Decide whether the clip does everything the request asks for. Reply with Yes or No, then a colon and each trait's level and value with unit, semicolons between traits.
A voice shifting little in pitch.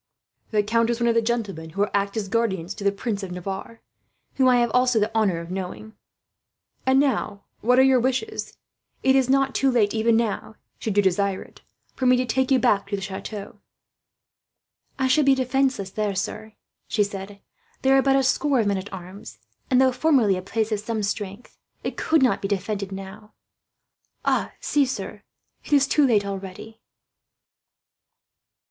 No: average, 4.3 semitones